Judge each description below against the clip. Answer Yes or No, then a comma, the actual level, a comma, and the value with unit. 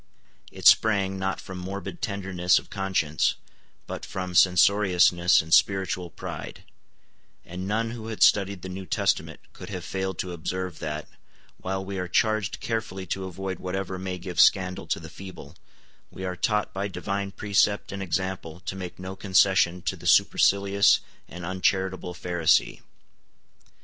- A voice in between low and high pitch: No, very low, 95 Hz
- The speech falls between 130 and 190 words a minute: Yes, average, 150 wpm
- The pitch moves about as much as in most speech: No, narrow, 1.4 semitones